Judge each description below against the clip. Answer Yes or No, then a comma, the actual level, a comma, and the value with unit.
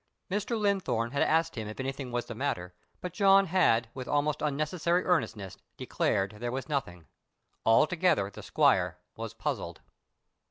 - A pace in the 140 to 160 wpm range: Yes, average, 150 wpm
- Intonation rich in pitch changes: Yes, wide, 7.6 semitones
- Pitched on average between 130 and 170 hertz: Yes, medium, 140 Hz